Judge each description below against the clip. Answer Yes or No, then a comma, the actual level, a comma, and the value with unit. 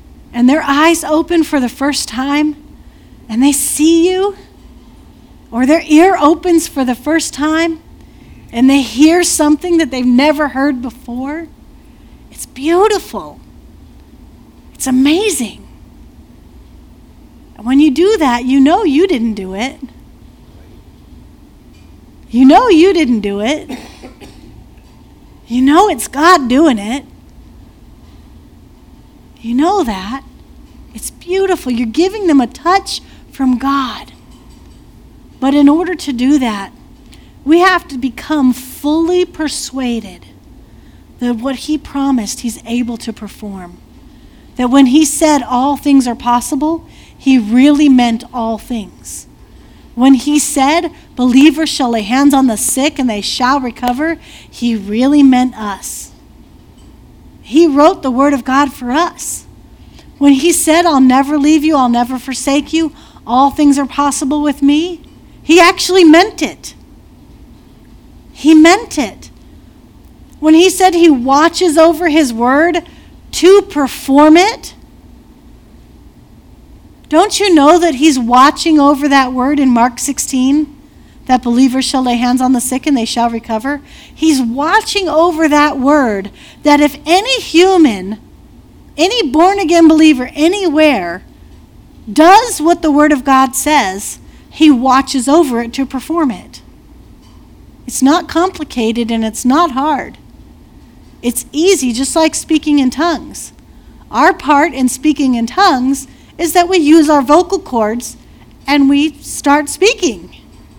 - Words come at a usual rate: No, slow, 130 wpm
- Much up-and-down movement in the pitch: No, average, 4.2 semitones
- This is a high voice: Yes, very high, 285 Hz